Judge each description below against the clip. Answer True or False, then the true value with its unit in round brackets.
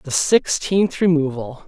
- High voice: False (155 Hz)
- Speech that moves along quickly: False (105 wpm)